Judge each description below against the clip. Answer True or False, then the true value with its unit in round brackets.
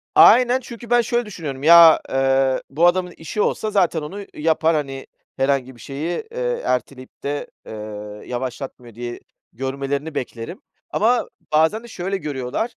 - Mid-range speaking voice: True (155 Hz)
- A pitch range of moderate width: False (7.0 semitones)